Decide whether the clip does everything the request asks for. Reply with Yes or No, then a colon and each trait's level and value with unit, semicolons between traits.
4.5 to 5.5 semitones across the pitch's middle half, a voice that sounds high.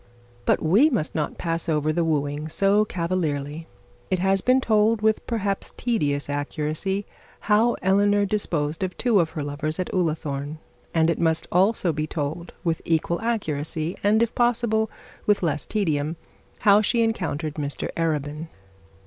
No: average, 5.2 semitones; medium, 170 Hz